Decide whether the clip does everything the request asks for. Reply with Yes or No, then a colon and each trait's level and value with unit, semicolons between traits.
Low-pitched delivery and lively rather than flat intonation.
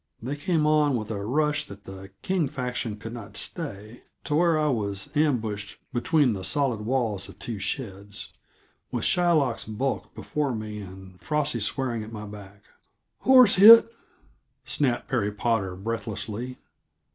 Yes: low, 115 Hz; wide, 6.1 semitones